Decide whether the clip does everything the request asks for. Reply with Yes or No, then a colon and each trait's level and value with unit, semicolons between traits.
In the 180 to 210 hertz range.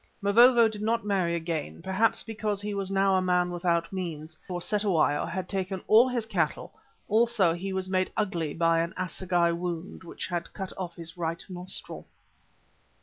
Yes: medium, 185 Hz